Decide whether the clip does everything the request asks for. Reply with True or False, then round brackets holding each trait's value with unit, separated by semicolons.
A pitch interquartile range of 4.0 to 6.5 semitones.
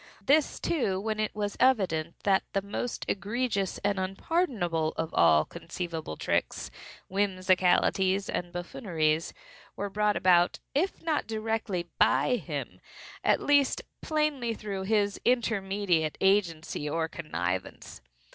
True (4.5 semitones)